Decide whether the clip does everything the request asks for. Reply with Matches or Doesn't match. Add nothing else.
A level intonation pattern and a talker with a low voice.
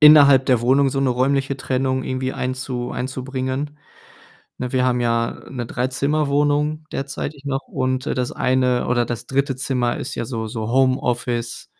Matches